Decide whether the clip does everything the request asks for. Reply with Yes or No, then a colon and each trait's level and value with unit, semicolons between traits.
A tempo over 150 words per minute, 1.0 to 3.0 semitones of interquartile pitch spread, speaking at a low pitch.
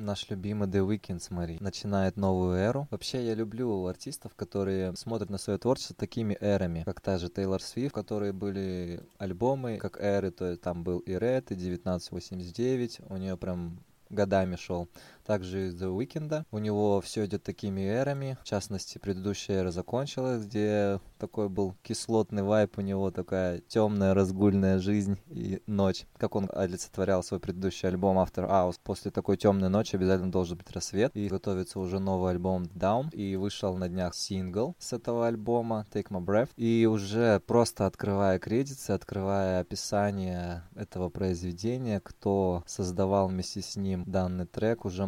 Yes: fast, 160 wpm; narrow, 2.4 semitones; low, 100 Hz